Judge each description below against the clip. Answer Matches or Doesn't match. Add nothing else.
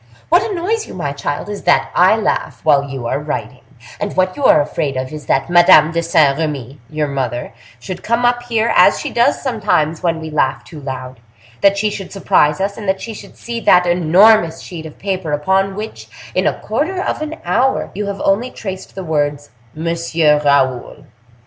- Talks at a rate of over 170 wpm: Matches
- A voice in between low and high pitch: Matches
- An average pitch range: Doesn't match